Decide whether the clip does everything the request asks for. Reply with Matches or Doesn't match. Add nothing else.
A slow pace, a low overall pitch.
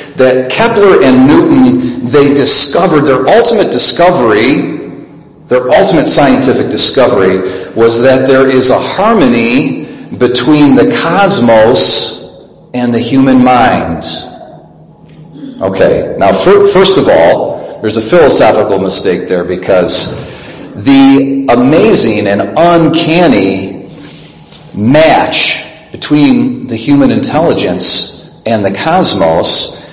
Doesn't match